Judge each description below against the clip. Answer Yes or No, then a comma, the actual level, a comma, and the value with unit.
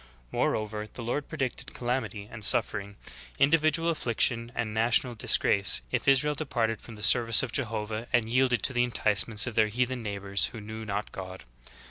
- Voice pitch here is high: No, low, 115 Hz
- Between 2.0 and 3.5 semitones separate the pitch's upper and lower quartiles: Yes, average, 3.0 semitones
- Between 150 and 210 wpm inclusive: Yes, average, 170 wpm